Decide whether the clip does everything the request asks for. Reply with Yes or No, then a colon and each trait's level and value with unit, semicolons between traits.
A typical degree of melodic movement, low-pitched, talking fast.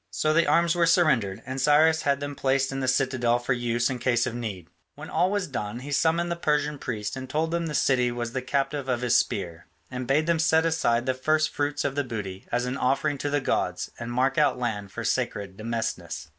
Yes: average, 3.8 semitones; low, 130 Hz; fast, 230 wpm